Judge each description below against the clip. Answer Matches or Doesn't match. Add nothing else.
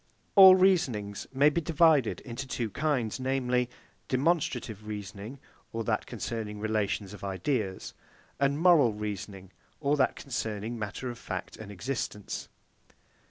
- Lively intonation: Doesn't match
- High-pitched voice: Doesn't match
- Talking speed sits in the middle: Doesn't match